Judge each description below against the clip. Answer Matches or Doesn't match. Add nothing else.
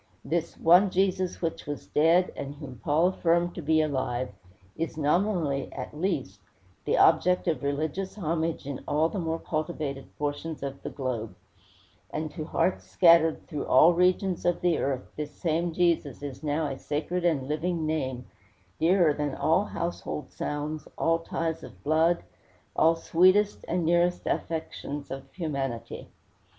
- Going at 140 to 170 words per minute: Matches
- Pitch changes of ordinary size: Matches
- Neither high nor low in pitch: Matches